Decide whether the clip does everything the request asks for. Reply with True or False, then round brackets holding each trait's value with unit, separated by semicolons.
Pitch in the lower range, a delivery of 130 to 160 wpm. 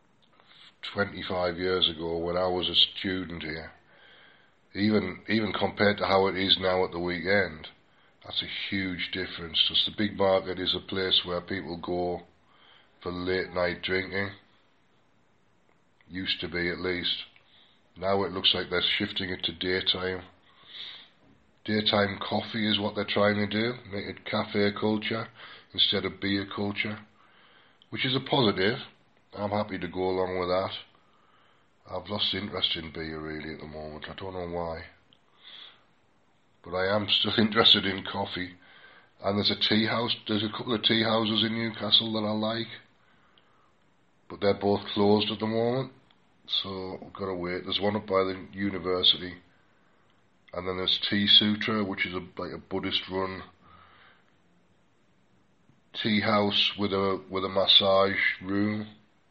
True (95 Hz; 155 wpm)